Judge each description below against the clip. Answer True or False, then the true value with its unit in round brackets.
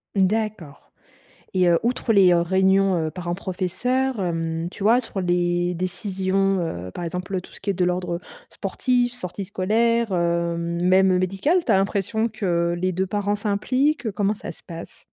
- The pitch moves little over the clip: False (3.1 semitones)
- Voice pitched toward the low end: False (190 Hz)